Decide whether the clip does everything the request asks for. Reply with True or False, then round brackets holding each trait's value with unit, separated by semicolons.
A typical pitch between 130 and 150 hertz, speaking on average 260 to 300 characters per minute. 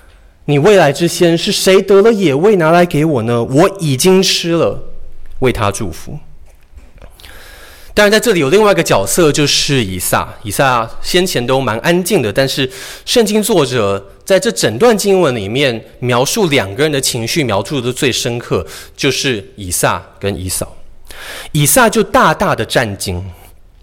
False (135 Hz; 235 characters per minute)